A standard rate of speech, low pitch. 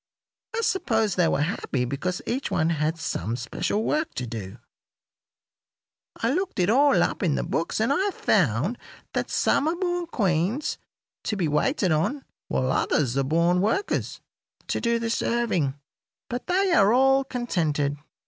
No: average, 160 wpm; high, 205 Hz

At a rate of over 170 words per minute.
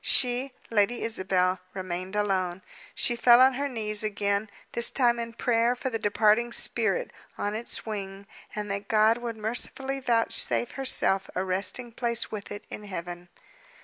No: average, 155 wpm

